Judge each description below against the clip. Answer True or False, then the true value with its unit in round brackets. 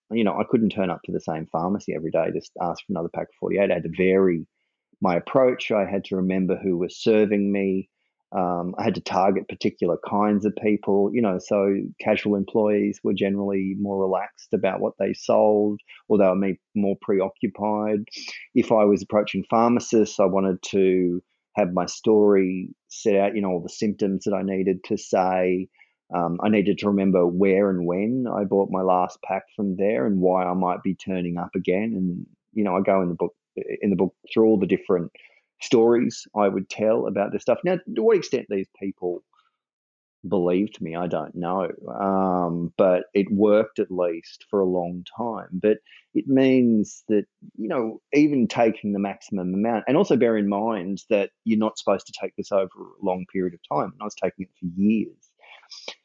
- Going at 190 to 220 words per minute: True (200 wpm)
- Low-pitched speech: True (100 Hz)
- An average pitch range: False (2.3 semitones)